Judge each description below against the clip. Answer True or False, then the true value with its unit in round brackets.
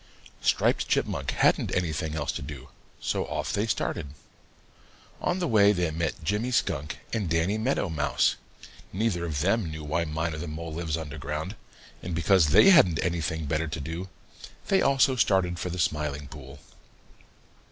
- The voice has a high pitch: False (85 Hz)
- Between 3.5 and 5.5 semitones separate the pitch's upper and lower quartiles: True (4.0 semitones)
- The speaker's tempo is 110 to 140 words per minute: False (165 wpm)